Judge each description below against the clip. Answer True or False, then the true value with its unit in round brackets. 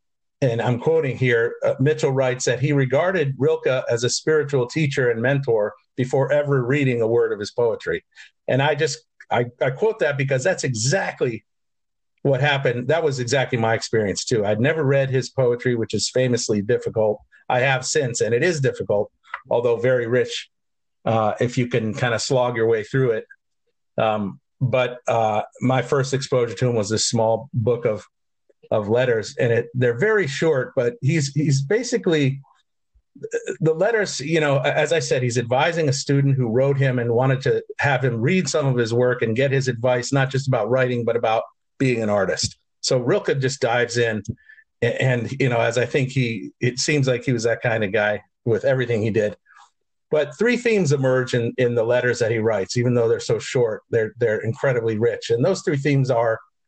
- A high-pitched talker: False (130 Hz)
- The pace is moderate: True (195 wpm)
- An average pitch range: True (4.3 semitones)